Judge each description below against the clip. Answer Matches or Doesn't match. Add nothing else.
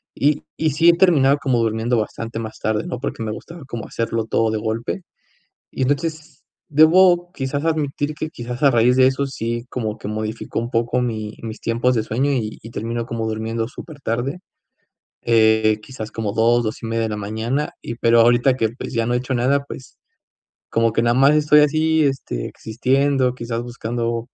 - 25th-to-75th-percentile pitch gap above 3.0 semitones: Matches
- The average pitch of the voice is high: Doesn't match